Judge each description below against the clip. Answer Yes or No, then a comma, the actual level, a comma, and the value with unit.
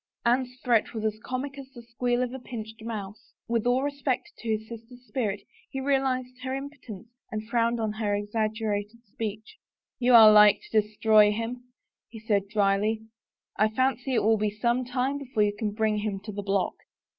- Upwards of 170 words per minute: Yes, average, 190 wpm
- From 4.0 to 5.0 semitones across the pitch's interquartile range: No, average, 2.8 semitones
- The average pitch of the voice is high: Yes, high, 225 Hz